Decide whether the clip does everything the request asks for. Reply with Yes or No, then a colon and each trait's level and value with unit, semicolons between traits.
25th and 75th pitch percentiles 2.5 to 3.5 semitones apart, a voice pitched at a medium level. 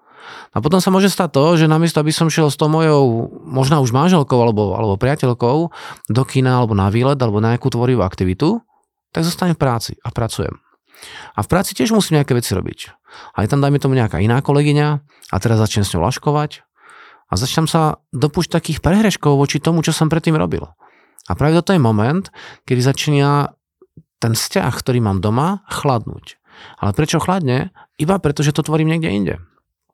No: average, 5.3 semitones; medium, 145 Hz